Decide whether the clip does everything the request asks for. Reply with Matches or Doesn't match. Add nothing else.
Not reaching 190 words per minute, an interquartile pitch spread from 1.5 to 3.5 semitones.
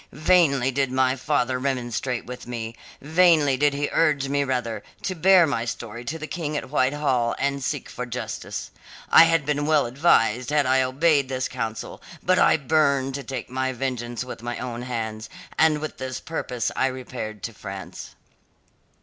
Matches